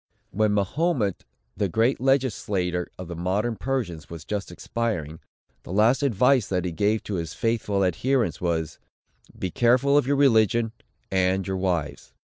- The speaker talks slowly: No, average, 150 wpm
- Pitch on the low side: Yes, low, 105 Hz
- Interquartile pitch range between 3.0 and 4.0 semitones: No, average, 5.1 semitones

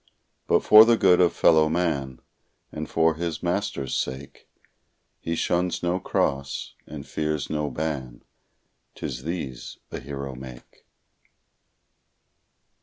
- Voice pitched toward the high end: No, very low, 75 Hz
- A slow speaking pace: Yes, slow, 115 wpm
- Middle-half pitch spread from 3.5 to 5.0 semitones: Yes, average, 4.2 semitones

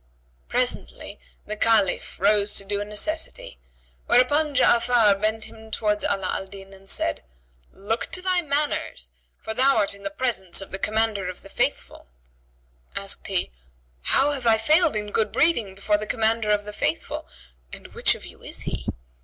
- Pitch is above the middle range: Yes, high, 210 Hz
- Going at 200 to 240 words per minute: No, average, 175 wpm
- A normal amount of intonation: Yes, average, 3.5 semitones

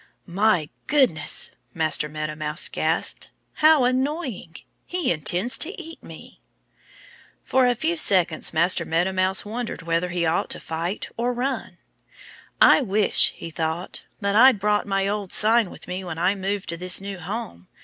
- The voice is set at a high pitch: Yes, high, 195 Hz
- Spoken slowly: No, average, 160 wpm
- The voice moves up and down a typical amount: No, wide, 6.0 semitones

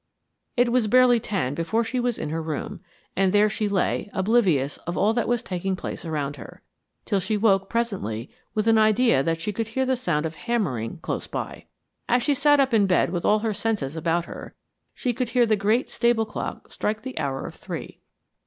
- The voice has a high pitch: Yes, high, 210 Hz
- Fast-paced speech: Yes, fast, 210 wpm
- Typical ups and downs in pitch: No, wide, 5.8 semitones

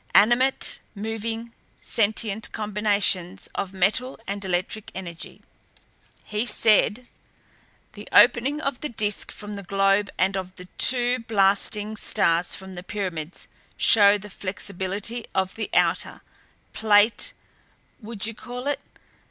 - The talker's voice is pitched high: Yes, high, 210 Hz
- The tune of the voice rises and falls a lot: No, average, 2.8 semitones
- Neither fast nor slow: No, slow, 120 wpm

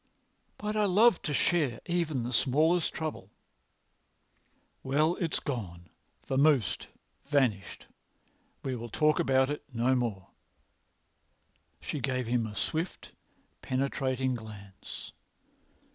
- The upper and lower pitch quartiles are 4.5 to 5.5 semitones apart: Yes, average, 4.8 semitones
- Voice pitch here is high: No, low, 130 Hz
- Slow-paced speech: Yes, slow, 100 wpm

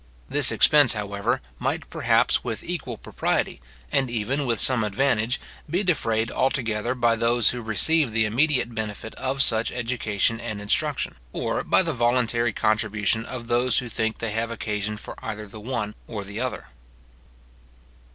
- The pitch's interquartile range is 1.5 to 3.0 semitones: Yes, average, 2.7 semitones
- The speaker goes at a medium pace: Yes, average, 155 wpm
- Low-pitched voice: Yes, low, 115 Hz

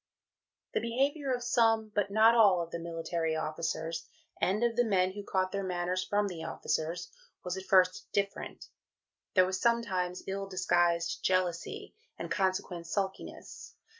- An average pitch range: Yes, average, 3.3 semitones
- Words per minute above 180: No, average, 150 wpm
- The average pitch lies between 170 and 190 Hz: Yes, medium, 185 Hz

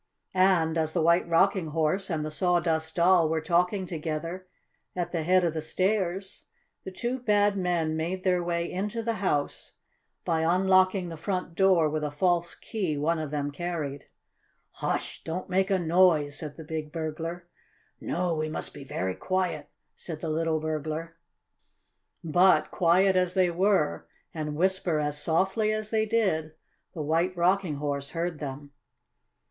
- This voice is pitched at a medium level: Yes, medium, 170 Hz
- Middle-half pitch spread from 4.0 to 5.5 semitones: No, average, 3.0 semitones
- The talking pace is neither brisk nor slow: Yes, average, 160 wpm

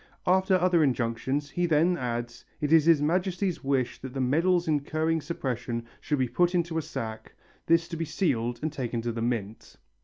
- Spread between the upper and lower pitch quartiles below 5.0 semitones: No, wide, 5.6 semitones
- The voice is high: No, medium, 150 Hz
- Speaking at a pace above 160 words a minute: Yes, average, 185 wpm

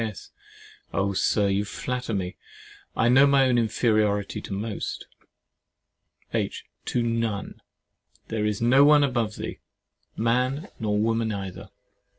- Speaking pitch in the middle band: No, low, 115 Hz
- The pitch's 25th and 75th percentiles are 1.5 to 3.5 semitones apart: Yes, average, 3.2 semitones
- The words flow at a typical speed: No, slow, 130 wpm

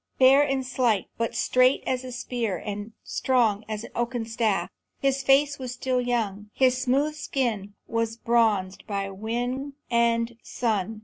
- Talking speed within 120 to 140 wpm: No, average, 150 wpm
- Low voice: No, high, 235 Hz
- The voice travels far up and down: No, average, 2.9 semitones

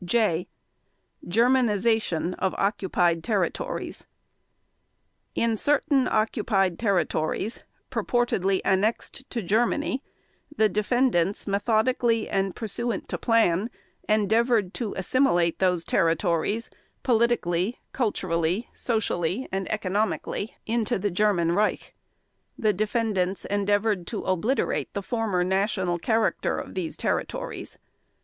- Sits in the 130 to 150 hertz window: No, high, 205 Hz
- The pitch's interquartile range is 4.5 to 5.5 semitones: No, average, 3.9 semitones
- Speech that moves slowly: Yes, slow, 100 wpm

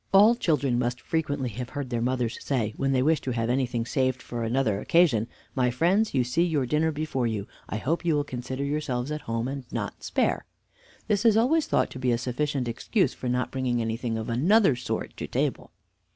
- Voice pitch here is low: Yes, low, 130 Hz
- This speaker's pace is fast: Yes, fast, 210 wpm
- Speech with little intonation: No, average, 4.0 semitones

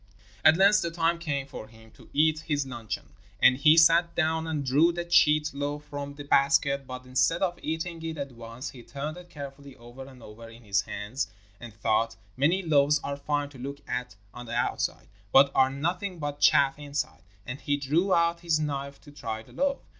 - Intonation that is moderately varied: Yes, average, 4.0 semitones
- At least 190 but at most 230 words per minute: Yes, fast, 205 wpm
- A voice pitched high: No, medium, 145 Hz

